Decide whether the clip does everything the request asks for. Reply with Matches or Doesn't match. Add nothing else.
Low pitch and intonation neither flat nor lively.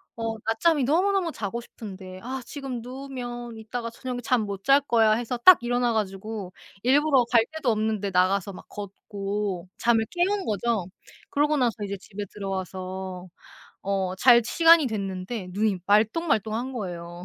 Doesn't match